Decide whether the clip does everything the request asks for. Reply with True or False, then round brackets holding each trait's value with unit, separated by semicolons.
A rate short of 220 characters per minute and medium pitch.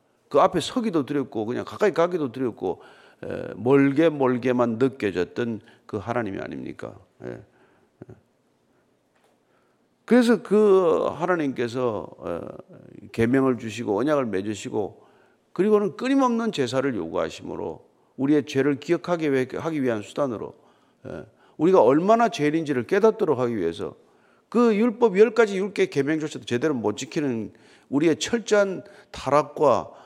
False (285 characters per minute; 145 Hz)